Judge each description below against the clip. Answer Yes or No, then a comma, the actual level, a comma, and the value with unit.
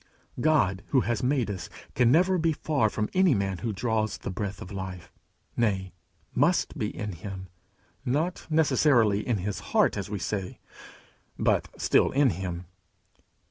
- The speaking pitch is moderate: No, low, 110 Hz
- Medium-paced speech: Yes, average, 155 wpm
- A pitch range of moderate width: No, wide, 6.4 semitones